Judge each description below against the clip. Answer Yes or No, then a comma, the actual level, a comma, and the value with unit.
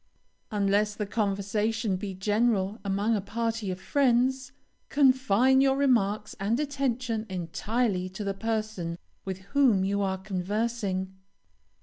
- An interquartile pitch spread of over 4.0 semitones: No, average, 3.5 semitones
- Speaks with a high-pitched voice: Yes, high, 210 Hz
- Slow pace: Yes, slow, 120 wpm